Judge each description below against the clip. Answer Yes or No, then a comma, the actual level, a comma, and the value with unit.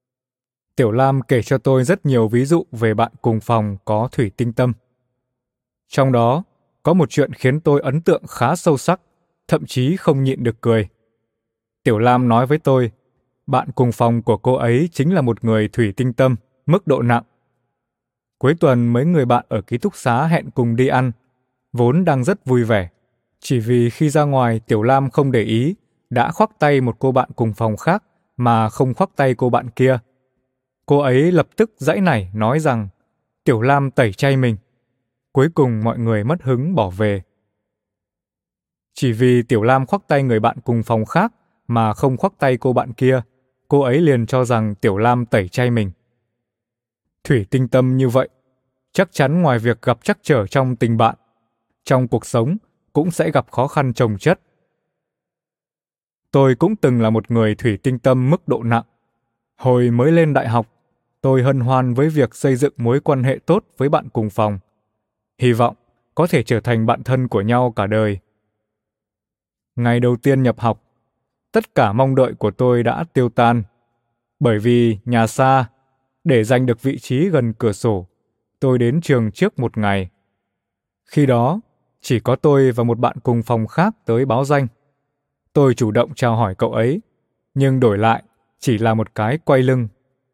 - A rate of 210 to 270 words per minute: No, average, 185 wpm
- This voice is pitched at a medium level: No, low, 125 Hz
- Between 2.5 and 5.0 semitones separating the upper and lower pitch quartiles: Yes, average, 2.8 semitones